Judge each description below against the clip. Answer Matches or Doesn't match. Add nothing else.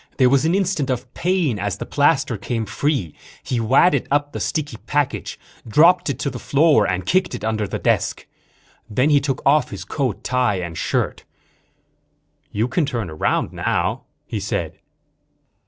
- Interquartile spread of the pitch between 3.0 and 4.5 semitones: Doesn't match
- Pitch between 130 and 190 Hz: Matches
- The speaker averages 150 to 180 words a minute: Matches